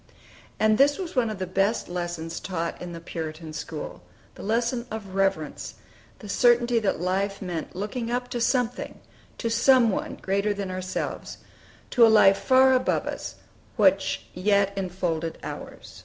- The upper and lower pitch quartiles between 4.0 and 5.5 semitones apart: Yes, average, 4.6 semitones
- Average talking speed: Yes, average, 155 wpm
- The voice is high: Yes, high, 200 Hz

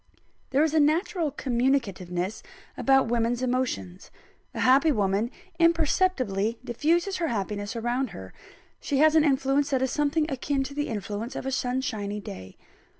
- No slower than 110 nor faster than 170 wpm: Yes, average, 150 wpm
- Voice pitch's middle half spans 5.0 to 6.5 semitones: Yes, average, 5.3 semitones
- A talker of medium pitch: No, very high, 260 Hz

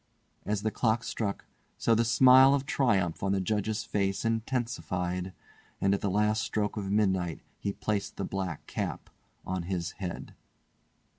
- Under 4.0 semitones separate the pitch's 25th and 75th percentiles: Yes, average, 2.9 semitones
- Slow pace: No, average, 155 wpm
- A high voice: No, low, 100 Hz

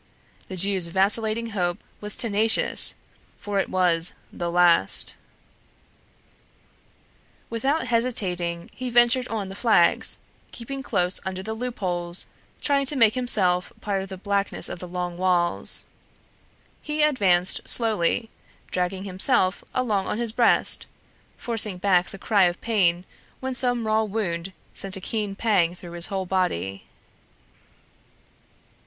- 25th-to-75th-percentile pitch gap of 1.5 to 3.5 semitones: No, average, 4.2 semitones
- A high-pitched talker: Yes, high, 195 Hz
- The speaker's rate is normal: No, slow, 130 wpm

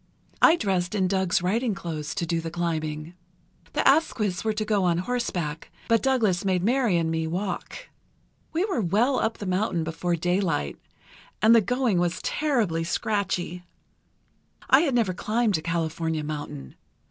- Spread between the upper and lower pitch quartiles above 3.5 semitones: Yes, average, 5.1 semitones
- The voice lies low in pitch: No, medium, 185 Hz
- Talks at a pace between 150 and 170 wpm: Yes, average, 160 wpm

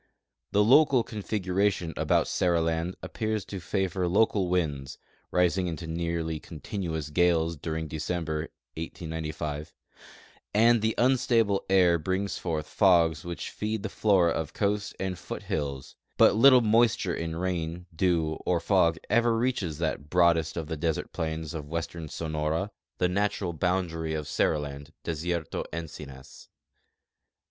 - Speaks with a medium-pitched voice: No, very low, 85 Hz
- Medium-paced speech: No, slow, 130 wpm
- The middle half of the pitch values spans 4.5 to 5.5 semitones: No, average, 3.5 semitones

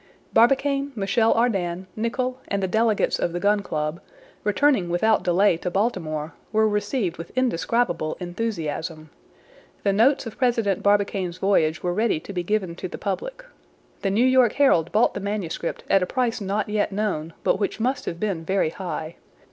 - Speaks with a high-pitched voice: Yes, high, 200 Hz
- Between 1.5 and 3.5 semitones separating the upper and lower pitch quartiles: No, average, 4.6 semitones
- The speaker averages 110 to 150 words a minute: No, average, 170 wpm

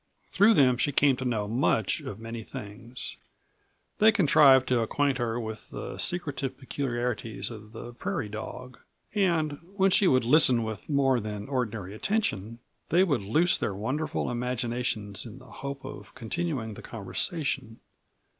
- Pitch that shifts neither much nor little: Yes, average, 4.4 semitones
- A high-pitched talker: No, low, 125 Hz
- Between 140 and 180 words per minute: Yes, average, 150 wpm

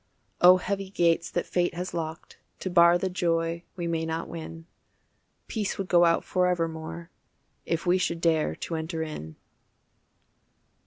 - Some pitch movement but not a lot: No, narrow, 1.6 semitones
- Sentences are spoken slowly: No, average, 150 wpm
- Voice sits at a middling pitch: Yes, medium, 170 Hz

